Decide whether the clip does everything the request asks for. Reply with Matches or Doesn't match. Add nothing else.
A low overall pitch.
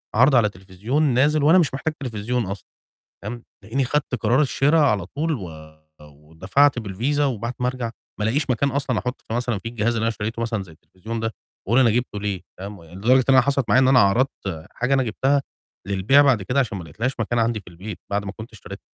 Matches